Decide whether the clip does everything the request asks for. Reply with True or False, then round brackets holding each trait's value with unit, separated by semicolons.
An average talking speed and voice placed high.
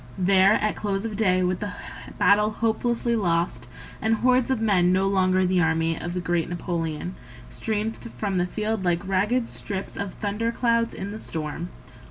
True (180 wpm; 195 Hz)